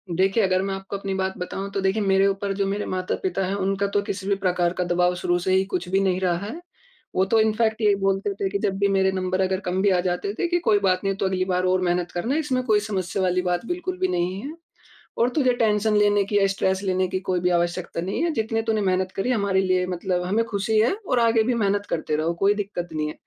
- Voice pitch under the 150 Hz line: No, high, 195 Hz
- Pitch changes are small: Yes, narrow, 2.1 semitones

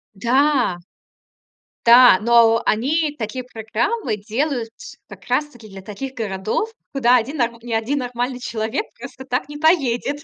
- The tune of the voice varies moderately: Yes, average, 4.0 semitones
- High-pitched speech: Yes, high, 245 Hz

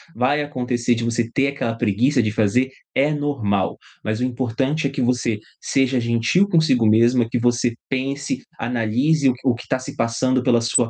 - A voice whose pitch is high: No, low, 125 Hz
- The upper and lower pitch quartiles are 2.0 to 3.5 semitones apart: Yes, average, 2.7 semitones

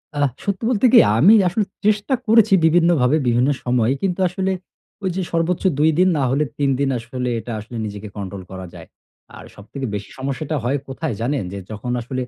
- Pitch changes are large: Yes, wide, 6.8 semitones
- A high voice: No, medium, 140 Hz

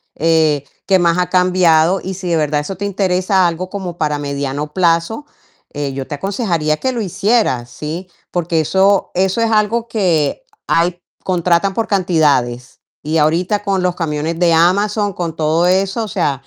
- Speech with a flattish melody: No, average, 3.7 semitones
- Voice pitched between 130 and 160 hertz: No, medium, 175 Hz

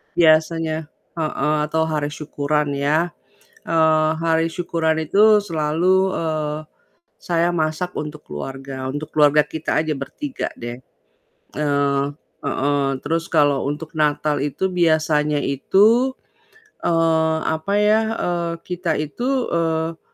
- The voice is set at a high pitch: No, medium, 160 Hz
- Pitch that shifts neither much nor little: No, narrow, 2.1 semitones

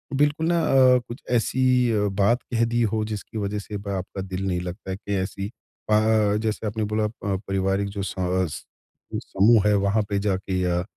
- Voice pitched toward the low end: Yes, low, 105 Hz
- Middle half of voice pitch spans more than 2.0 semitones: Yes, narrow, 2.5 semitones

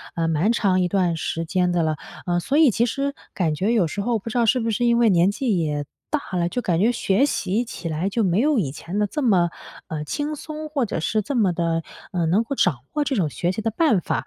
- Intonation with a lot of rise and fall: Yes, wide, 5.7 semitones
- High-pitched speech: Yes, high, 200 Hz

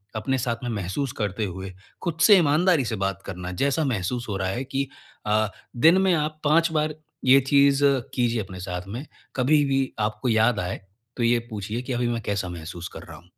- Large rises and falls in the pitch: Yes, wide, 6.3 semitones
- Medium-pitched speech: No, low, 120 Hz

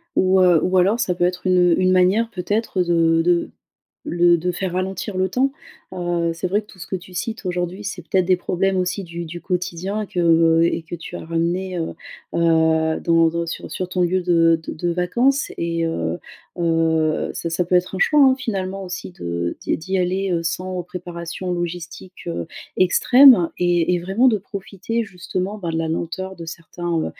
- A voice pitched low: No, medium, 180 Hz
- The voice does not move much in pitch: Yes, narrow, 2.0 semitones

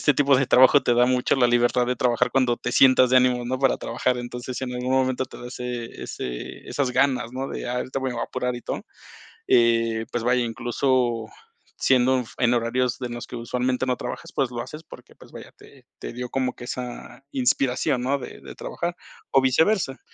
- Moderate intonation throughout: No, narrow, 1.3 semitones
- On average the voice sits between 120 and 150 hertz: Yes, low, 125 Hz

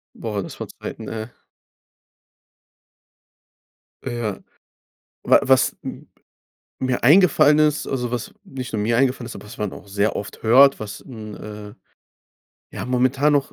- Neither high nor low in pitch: No, low, 120 Hz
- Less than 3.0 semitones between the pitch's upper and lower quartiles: No, average, 3.9 semitones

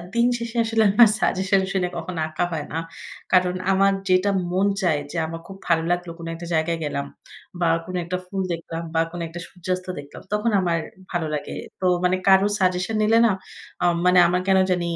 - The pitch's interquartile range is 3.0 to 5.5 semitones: No, narrow, 2.4 semitones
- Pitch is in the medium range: Yes, medium, 180 Hz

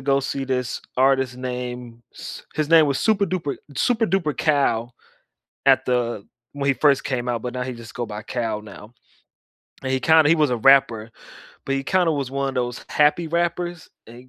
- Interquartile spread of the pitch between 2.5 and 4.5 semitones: Yes, average, 3.7 semitones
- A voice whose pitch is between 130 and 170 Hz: Yes, low, 135 Hz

